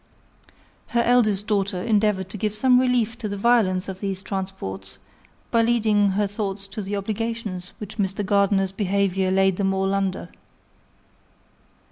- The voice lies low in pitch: No, high, 200 Hz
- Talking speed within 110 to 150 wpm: Yes, average, 145 wpm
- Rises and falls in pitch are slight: Yes, narrow, 2.1 semitones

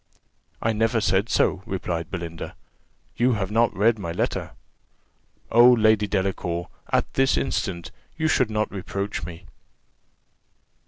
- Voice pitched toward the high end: No, low, 105 Hz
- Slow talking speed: Yes, slow, 125 wpm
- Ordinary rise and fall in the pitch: Yes, average, 3.6 semitones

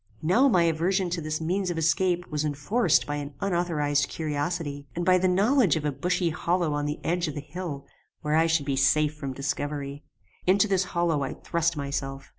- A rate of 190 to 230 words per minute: Yes, average, 200 wpm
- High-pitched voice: No, medium, 160 Hz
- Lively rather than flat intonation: No, average, 3.6 semitones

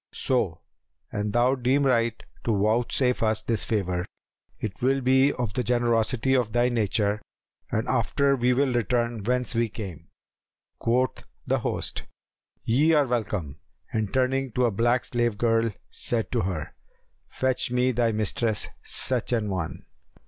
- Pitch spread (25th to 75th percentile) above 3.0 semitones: No, average, 2.7 semitones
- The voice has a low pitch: Yes, low, 120 Hz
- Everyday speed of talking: Yes, average, 150 wpm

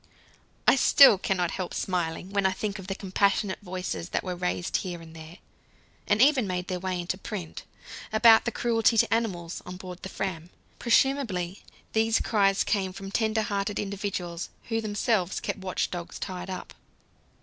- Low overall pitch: No, high, 190 Hz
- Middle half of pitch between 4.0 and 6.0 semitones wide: No, average, 3.1 semitones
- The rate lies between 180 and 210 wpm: No, average, 170 wpm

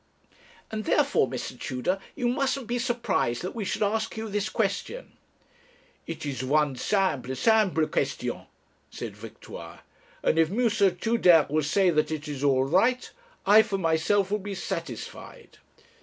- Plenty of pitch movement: Yes, wide, 6.3 semitones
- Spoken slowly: No, average, 150 wpm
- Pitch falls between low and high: No, high, 195 Hz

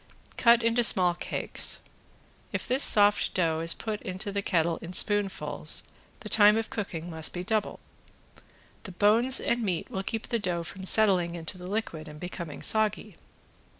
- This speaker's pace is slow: No, average, 165 wpm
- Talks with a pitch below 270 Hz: Yes, high, 190 Hz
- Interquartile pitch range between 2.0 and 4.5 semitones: Yes, average, 4.1 semitones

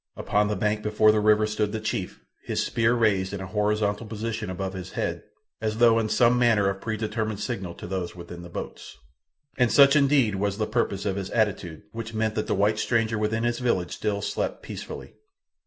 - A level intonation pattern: Yes, narrow, 2.2 semitones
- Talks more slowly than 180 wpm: No, average, 200 wpm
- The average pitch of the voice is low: Yes, low, 105 Hz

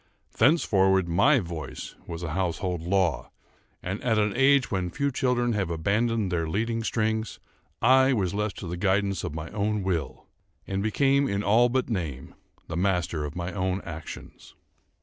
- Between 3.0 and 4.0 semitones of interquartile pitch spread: No, average, 4.7 semitones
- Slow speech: No, average, 165 wpm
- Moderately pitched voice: No, low, 100 Hz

